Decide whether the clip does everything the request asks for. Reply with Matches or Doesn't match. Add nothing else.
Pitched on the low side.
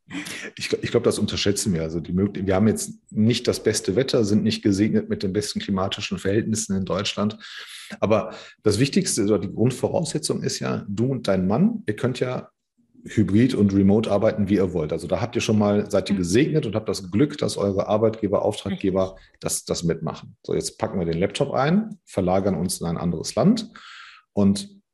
Matches